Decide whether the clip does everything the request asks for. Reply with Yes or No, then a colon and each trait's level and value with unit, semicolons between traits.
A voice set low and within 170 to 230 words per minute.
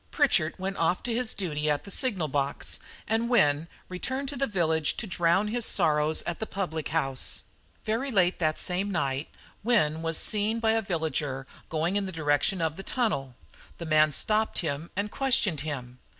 No: medium, 175 Hz; average, 180 wpm